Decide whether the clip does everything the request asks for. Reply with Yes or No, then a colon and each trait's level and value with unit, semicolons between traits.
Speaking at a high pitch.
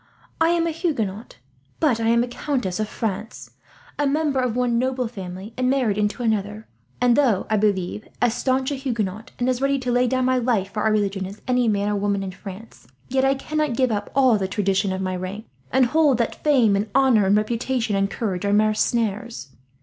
Yes: high, 225 Hz